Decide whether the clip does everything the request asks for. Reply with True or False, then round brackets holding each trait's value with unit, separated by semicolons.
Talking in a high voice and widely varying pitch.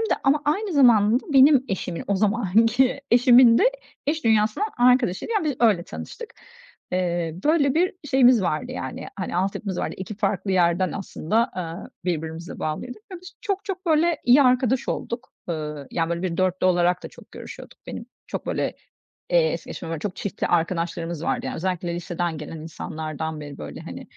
True (200 Hz; 7.3 semitones)